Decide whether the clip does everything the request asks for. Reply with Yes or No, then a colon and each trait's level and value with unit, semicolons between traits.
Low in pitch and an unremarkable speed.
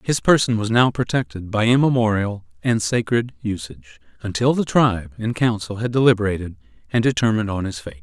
Yes: low, 110 Hz; average, 165 wpm